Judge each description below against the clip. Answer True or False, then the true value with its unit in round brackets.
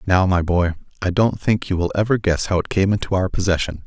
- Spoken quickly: True (250 wpm)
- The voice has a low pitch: True (95 Hz)